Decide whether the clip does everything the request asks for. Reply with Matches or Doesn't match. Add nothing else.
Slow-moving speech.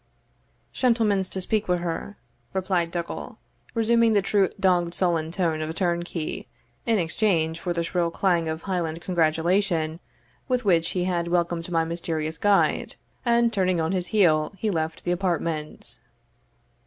Doesn't match